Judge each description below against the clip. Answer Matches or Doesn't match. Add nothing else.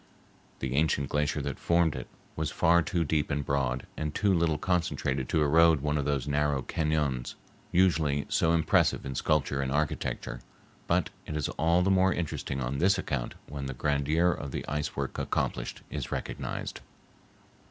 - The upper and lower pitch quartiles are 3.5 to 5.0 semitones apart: Doesn't match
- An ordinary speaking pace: Matches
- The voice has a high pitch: Doesn't match